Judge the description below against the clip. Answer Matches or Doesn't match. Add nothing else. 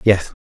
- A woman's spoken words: Doesn't match